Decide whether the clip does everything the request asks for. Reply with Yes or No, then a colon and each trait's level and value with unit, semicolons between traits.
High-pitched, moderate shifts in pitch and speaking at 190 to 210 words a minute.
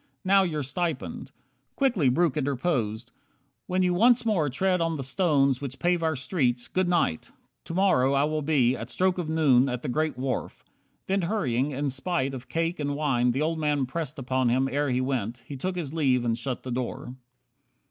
No: medium, 140 Hz; average, 4.9 semitones; average, 200 wpm